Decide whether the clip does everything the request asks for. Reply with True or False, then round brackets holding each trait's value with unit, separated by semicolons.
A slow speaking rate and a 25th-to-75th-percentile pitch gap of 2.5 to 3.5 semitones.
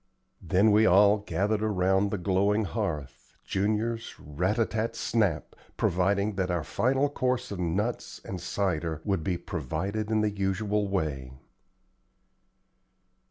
True (130 wpm; 3.1 semitones)